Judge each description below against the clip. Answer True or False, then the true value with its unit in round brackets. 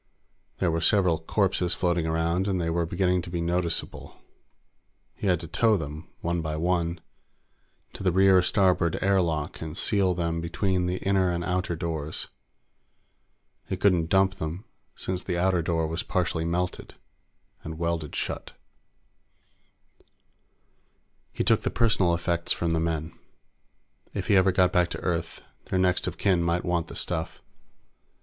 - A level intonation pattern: True (1.9 semitones)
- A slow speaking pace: False (155 wpm)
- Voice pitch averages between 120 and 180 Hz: False (85 Hz)